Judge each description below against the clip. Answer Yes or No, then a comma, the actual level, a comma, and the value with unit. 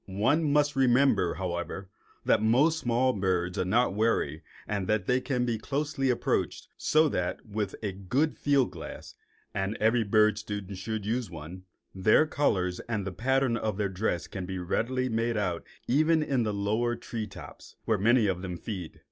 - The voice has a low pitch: Yes, low, 110 Hz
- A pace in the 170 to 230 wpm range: Yes, average, 175 wpm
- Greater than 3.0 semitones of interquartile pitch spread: Yes, average, 5.0 semitones